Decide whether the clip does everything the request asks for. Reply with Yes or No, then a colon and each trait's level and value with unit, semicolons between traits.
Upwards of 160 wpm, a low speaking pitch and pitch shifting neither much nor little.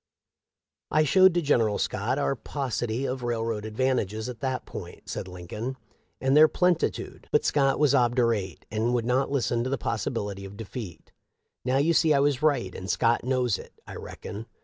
Yes: average, 180 wpm; low, 125 Hz; average, 3.9 semitones